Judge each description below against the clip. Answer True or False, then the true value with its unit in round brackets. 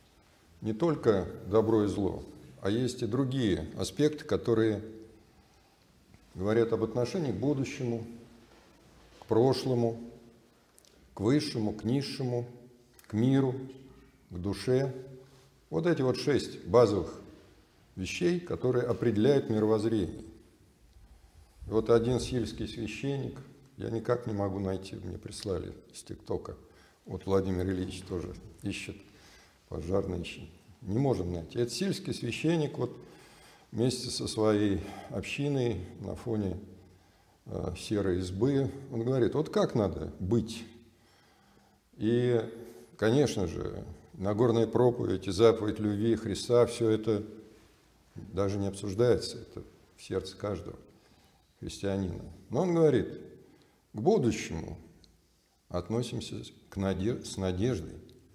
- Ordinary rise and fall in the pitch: True (3.9 semitones)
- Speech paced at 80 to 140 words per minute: True (110 wpm)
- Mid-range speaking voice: False (110 Hz)